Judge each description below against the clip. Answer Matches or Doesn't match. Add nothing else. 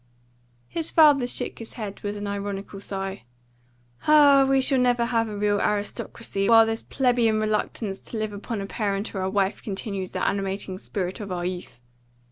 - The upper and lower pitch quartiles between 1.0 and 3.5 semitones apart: Matches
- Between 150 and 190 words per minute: Matches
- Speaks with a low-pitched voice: Doesn't match